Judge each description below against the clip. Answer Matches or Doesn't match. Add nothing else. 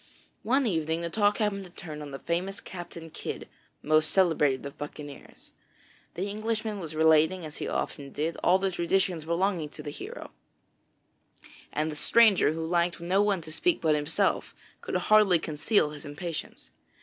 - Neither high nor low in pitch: Matches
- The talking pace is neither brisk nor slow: Matches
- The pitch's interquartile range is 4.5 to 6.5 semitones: Doesn't match